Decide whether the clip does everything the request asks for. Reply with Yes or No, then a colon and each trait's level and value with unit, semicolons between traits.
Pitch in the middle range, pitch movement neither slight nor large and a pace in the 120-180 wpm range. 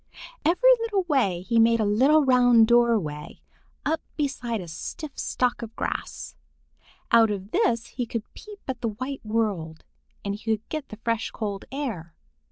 No: high, 230 Hz; average, 4.6 semitones; average, 165 wpm